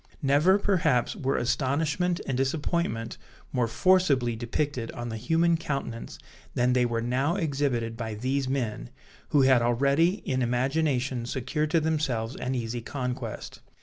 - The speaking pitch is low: Yes, low, 130 Hz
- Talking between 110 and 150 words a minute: Yes, average, 140 wpm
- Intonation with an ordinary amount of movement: Yes, average, 4.2 semitones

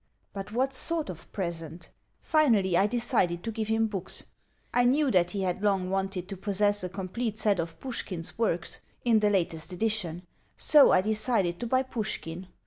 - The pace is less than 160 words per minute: No, average, 175 wpm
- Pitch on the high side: Yes, high, 200 Hz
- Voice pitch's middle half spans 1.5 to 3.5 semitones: No, average, 4.2 semitones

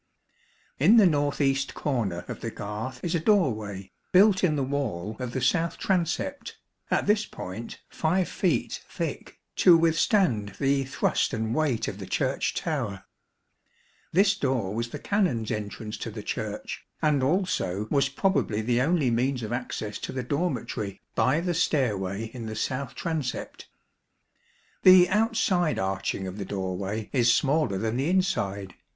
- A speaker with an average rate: Yes, average, 155 wpm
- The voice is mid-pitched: No, low, 130 Hz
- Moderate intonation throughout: No, wide, 7.8 semitones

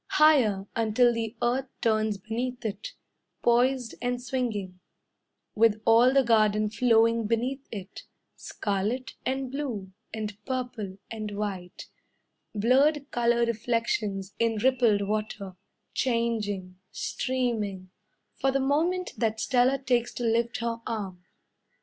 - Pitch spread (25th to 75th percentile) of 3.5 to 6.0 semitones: No, average, 3.1 semitones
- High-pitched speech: Yes, high, 230 Hz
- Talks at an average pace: No, slow, 115 wpm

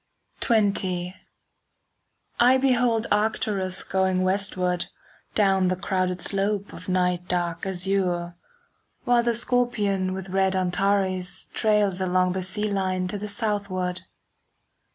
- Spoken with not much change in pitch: Yes, narrow, 2.2 semitones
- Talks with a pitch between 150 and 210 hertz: Yes, high, 190 Hz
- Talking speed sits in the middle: No, slow, 110 wpm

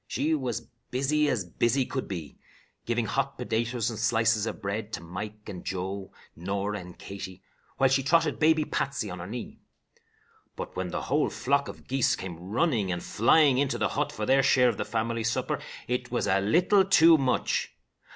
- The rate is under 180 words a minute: No, average, 185 wpm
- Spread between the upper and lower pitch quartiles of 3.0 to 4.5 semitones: No, wide, 5.4 semitones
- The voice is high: No, low, 115 Hz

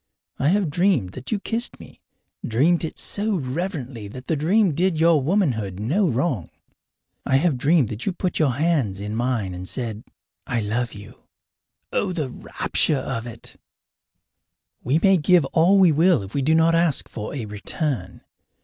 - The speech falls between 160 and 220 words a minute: Yes, average, 170 wpm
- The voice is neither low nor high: Yes, medium, 145 Hz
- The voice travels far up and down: Yes, wide, 6.9 semitones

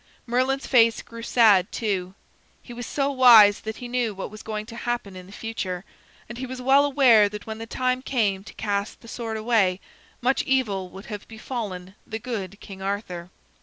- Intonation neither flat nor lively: Yes, average, 3.6 semitones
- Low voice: No, high, 220 Hz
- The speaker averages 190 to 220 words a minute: Yes, average, 195 wpm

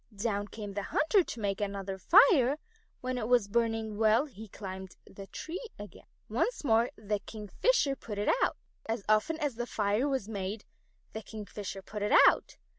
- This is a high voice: Yes, high, 220 Hz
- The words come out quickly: No, average, 175 wpm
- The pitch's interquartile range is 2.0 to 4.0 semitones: Yes, average, 3.6 semitones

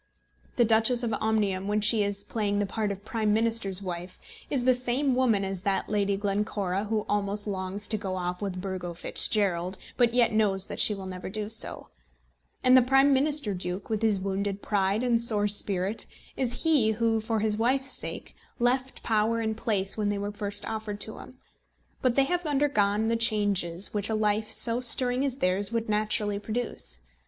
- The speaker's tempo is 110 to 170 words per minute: No, average, 190 wpm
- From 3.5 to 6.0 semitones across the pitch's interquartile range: No, average, 2.7 semitones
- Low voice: No, high, 210 Hz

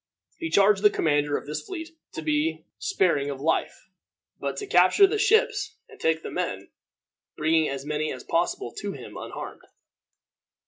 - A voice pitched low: No, medium, 165 Hz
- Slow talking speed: No, average, 165 wpm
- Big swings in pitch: Yes, wide, 6.5 semitones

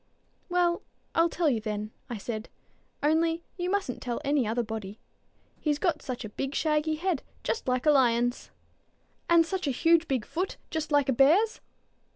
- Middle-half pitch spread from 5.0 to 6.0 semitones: Yes, wide, 5.5 semitones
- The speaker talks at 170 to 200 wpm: Yes, average, 175 wpm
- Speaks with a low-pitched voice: No, very high, 295 Hz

